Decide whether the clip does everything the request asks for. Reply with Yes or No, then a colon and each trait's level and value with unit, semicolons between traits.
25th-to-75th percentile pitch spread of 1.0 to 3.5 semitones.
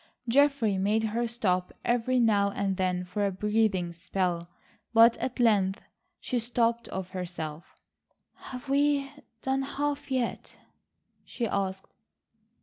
No: average, 4.5 semitones